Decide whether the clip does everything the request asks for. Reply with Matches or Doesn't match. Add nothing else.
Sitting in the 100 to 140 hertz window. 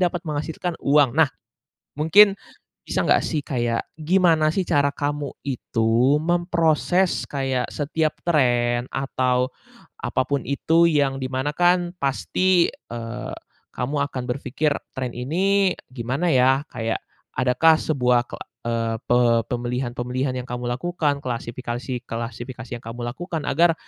Matches